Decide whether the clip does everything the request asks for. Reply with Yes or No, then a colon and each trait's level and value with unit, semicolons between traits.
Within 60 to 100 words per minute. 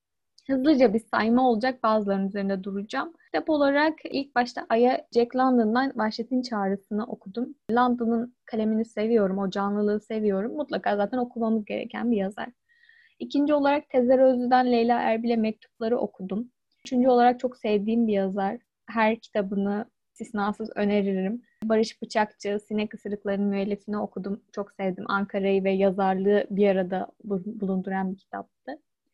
No: average, 130 wpm